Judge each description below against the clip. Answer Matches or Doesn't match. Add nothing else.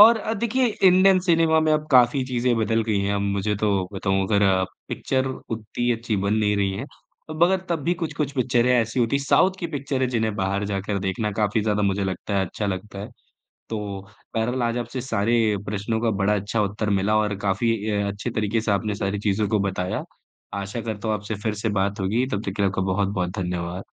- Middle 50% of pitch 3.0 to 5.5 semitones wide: Matches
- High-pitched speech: Doesn't match